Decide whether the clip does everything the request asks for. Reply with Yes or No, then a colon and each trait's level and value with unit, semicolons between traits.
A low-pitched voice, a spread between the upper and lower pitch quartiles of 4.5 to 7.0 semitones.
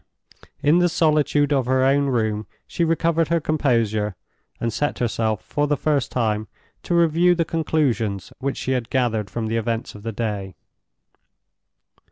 Yes: low, 130 Hz; wide, 5.6 semitones